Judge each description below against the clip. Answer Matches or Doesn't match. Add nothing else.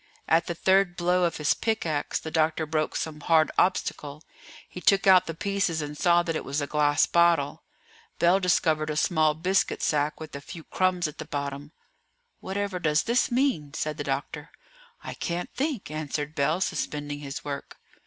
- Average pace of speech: Matches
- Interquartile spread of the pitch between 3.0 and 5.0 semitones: Matches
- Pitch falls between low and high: Matches